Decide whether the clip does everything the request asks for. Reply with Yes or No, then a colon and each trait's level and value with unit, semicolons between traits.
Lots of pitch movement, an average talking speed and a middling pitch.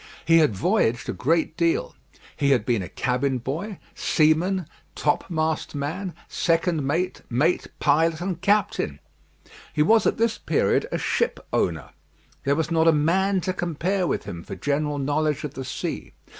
No: average, 4.0 semitones; average, 160 wpm; medium, 160 Hz